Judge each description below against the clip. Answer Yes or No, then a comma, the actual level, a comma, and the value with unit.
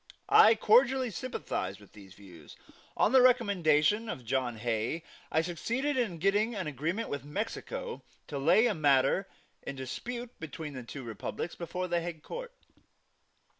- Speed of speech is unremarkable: Yes, average, 150 wpm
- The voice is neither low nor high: Yes, medium, 170 Hz